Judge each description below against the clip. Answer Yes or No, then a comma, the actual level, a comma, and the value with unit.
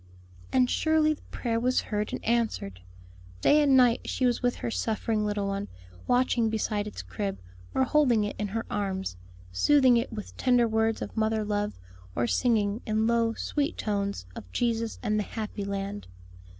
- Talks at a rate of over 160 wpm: Yes, average, 175 wpm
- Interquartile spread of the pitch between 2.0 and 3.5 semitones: Yes, average, 2.9 semitones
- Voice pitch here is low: No, high, 220 Hz